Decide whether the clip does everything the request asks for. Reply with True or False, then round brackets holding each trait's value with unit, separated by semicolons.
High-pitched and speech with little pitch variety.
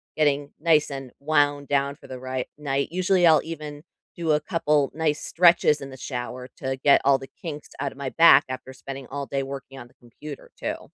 False (140 Hz; 2.3 semitones)